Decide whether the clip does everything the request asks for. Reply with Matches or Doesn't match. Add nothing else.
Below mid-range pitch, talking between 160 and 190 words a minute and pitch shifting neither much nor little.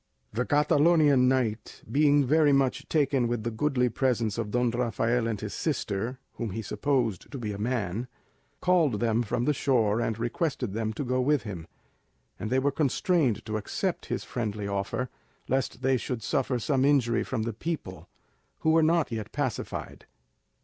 Matches